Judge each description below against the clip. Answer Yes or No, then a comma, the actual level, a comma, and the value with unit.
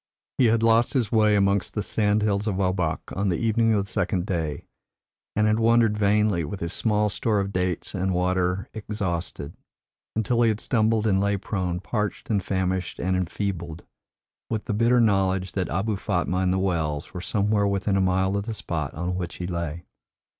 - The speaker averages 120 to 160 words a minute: No, average, 190 wpm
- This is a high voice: No, low, 100 Hz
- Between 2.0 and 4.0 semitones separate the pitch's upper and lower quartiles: Yes, average, 2.8 semitones